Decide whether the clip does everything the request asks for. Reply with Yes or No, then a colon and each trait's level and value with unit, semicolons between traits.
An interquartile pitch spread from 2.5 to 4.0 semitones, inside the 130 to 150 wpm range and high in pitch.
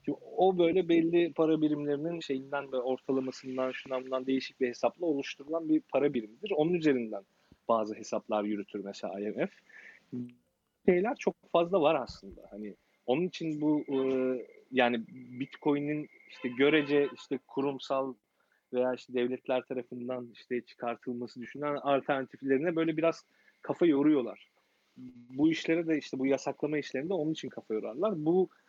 No: average, 3.3 semitones; average, 135 wpm; low, 135 Hz